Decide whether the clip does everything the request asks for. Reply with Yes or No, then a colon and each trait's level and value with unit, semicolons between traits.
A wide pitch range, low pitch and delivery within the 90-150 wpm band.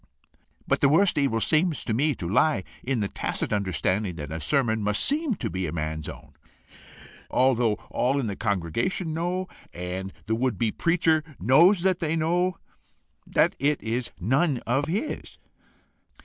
No: wide, 8.3 semitones; low, 125 Hz; average, 165 wpm